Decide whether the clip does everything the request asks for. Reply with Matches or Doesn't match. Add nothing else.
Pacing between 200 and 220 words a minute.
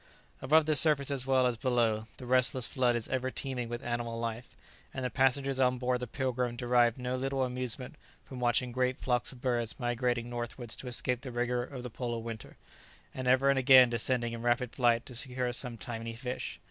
Matches